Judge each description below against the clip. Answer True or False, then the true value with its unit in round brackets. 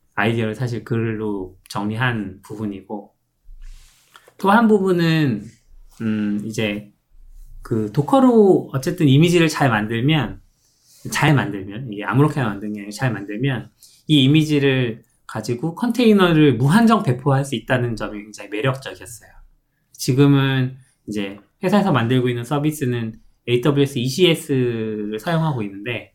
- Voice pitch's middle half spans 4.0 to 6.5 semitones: True (5.6 semitones)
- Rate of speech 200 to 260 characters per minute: False (290 characters per minute)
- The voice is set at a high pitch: False (125 Hz)